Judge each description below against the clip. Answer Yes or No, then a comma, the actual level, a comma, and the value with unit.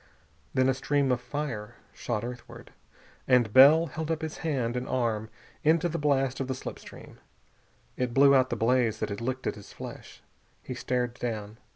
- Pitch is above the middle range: No, low, 130 Hz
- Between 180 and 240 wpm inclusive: Yes, average, 185 wpm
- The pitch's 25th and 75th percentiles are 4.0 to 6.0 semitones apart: No, average, 3.0 semitones